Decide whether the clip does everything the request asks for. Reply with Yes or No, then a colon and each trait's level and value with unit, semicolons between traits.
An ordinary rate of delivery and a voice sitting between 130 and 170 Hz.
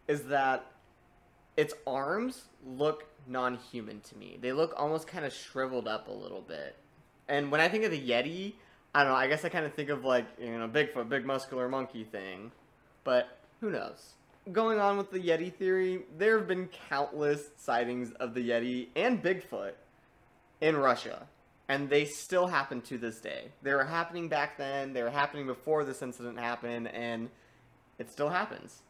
Yes: average, 185 wpm; medium, 140 Hz